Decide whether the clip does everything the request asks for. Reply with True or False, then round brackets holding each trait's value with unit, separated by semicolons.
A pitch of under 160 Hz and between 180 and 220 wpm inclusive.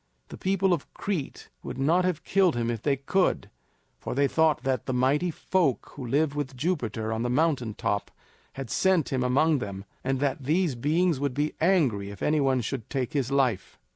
True (140 Hz; 200 wpm)